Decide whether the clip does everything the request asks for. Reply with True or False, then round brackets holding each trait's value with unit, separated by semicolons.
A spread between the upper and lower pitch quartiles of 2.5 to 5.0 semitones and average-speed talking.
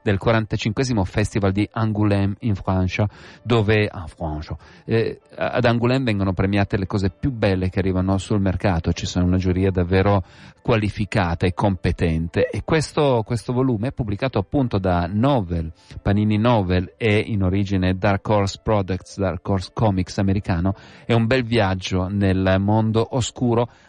True (3.2 semitones; 150 wpm)